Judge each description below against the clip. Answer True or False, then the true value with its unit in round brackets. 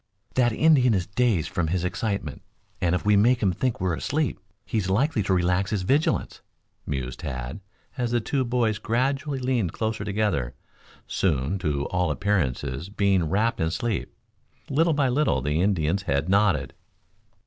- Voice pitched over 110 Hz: False (100 Hz)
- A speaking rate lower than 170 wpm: True (160 wpm)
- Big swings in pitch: True (6.1 semitones)